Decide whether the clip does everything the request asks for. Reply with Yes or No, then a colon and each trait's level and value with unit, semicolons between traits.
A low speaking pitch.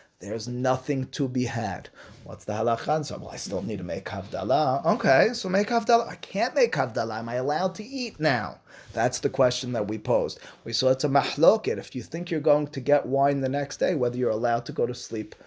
Yes: low, 130 Hz